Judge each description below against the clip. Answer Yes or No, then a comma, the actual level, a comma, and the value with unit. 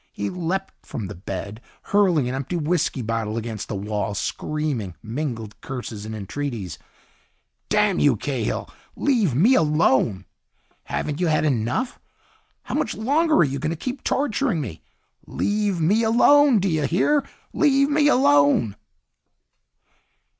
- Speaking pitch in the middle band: Yes, medium, 150 Hz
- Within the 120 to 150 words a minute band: Yes, average, 140 wpm